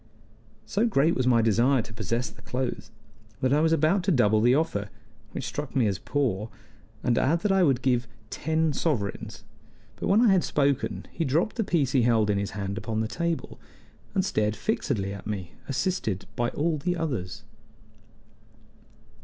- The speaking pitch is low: Yes, low, 130 Hz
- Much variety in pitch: Yes, wide, 6.9 semitones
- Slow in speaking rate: No, average, 180 wpm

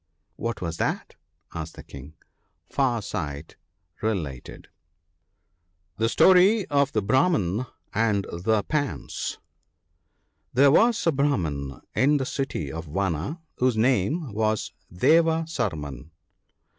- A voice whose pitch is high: No, low, 110 Hz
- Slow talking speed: Yes, slow, 120 wpm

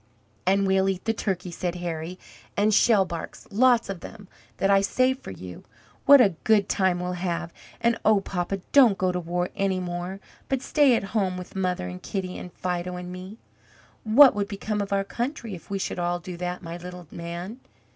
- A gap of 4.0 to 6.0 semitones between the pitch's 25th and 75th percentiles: No, average, 2.8 semitones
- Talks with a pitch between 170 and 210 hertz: Yes, high, 190 Hz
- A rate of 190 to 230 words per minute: Yes, average, 195 wpm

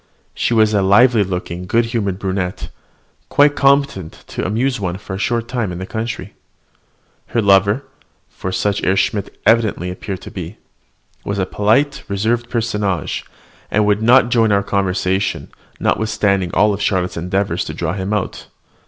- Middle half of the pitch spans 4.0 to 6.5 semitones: No, average, 3.3 semitones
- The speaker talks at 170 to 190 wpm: No, average, 155 wpm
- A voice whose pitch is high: No, low, 100 Hz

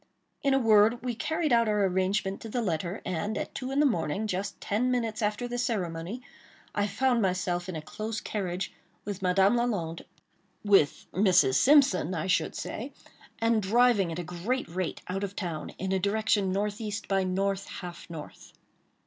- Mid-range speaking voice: No, high, 200 Hz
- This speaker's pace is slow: No, average, 170 wpm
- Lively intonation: No, average, 3.9 semitones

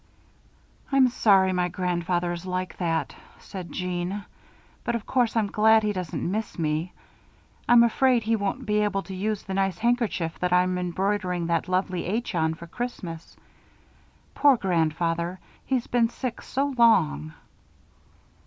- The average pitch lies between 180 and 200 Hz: Yes, high, 190 Hz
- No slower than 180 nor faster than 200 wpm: No, average, 150 wpm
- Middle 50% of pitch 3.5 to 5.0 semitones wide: Yes, average, 4.2 semitones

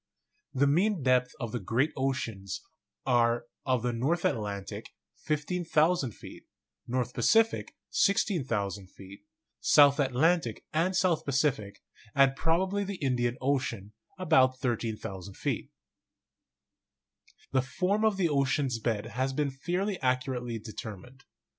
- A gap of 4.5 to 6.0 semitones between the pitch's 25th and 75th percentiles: Yes, wide, 5.4 semitones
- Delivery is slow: Yes, slow, 115 wpm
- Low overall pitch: Yes, low, 130 Hz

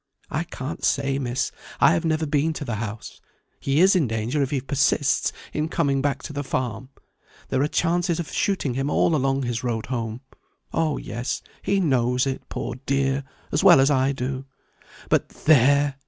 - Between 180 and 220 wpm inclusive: Yes, average, 185 wpm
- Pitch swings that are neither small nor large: Yes, average, 3.0 semitones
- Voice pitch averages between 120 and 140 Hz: Yes, low, 135 Hz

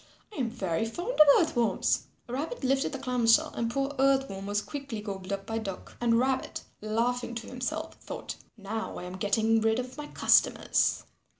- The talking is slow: No, average, 190 wpm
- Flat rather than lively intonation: No, average, 3.9 semitones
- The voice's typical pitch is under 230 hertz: No, high, 235 Hz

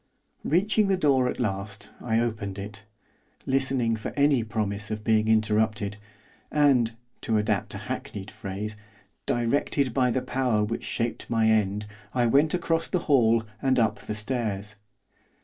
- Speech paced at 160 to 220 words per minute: No, average, 150 wpm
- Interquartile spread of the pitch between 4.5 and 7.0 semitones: No, average, 3.6 semitones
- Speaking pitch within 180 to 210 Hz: No, low, 115 Hz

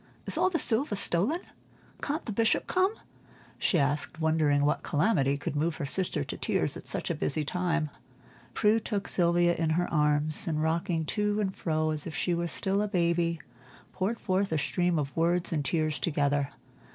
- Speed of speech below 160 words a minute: No, average, 185 wpm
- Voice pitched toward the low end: No, medium, 170 Hz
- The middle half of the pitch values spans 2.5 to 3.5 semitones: No, average, 4.0 semitones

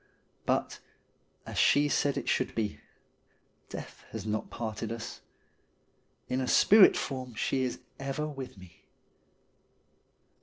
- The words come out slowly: Yes, slow, 120 wpm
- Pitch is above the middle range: No, low, 125 Hz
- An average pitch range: Yes, average, 3.9 semitones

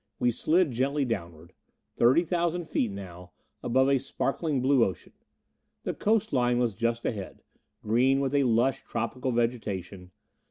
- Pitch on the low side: Yes, low, 125 Hz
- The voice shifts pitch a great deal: No, average, 4.0 semitones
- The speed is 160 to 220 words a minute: No, slow, 135 wpm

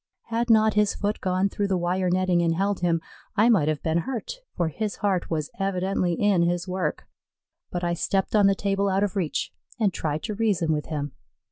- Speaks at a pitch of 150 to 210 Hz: Yes, medium, 185 Hz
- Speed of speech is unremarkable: No, fast, 210 wpm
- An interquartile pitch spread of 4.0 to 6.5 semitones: No, average, 3.1 semitones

